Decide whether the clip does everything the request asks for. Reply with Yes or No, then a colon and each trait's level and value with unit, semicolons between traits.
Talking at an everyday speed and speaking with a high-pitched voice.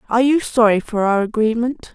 Yes: average, 185 wpm; high, 230 Hz